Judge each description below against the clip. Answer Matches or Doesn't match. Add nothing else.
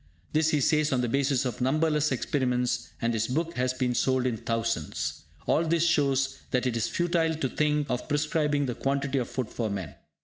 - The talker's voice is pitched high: Doesn't match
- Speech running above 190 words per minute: Matches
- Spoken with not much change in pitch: Doesn't match